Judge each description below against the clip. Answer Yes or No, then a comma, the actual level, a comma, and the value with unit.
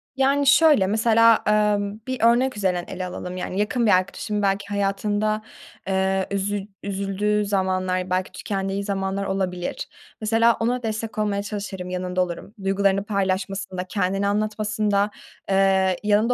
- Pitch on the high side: Yes, high, 200 Hz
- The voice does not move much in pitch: Yes, narrow, 1.9 semitones